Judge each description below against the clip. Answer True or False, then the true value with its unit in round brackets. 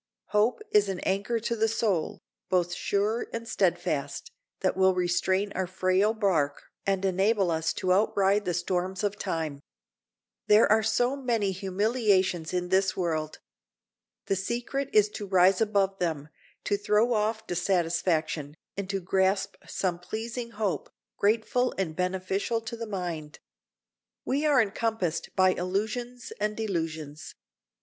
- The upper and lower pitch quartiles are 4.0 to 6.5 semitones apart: False (3.4 semitones)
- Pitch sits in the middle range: False (195 Hz)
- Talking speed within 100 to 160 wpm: True (140 wpm)